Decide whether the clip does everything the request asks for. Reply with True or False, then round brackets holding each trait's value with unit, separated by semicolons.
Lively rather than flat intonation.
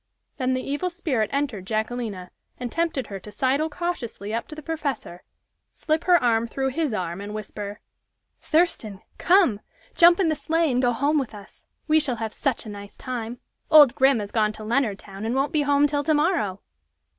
True (6.2 semitones)